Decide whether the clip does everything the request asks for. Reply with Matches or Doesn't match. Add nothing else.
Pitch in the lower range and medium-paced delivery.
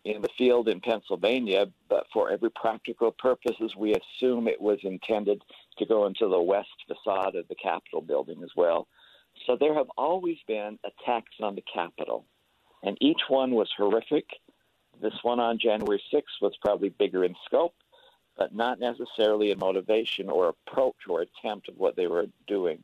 Matches